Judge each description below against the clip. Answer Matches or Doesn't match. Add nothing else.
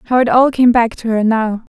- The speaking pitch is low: Doesn't match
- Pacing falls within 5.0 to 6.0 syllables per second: Matches